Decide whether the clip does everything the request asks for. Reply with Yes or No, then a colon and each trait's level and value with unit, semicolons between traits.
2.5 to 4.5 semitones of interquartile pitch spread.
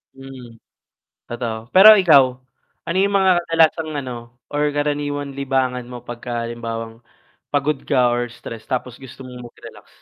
Yes: average, 3.3 semitones